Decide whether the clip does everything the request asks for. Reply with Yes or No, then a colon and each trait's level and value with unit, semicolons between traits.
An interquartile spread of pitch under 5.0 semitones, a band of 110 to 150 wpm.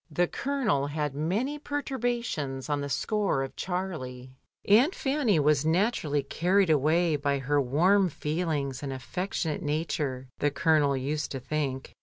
No: wide, 5.4 semitones; average, 140 wpm